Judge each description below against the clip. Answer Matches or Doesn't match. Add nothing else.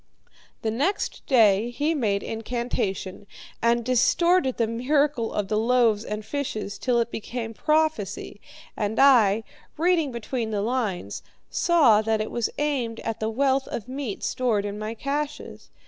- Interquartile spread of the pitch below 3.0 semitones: Doesn't match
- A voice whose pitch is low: Doesn't match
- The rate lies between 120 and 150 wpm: Matches